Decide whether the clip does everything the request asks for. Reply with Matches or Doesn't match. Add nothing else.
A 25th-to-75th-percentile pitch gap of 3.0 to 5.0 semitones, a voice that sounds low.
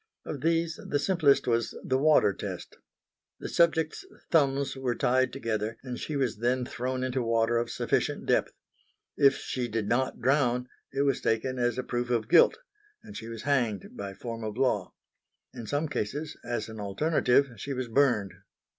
Matches